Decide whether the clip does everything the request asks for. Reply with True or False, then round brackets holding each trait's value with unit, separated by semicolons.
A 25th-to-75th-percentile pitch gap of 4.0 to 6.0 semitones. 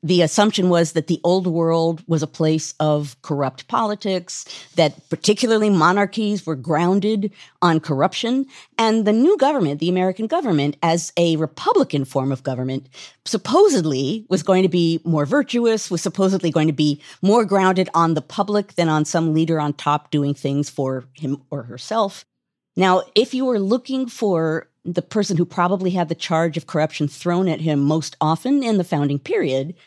True (4.7 semitones)